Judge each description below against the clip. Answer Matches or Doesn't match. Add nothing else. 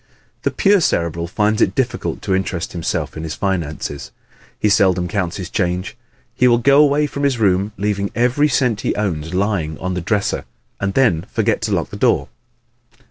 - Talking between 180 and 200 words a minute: Matches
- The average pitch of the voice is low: Matches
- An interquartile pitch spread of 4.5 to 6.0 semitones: Matches